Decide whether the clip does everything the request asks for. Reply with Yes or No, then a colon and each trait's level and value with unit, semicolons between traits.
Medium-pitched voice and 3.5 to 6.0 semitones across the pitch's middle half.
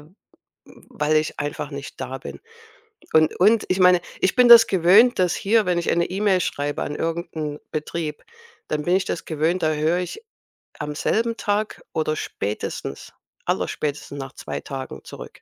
Yes: medium, 165 Hz; average, 4.1 semitones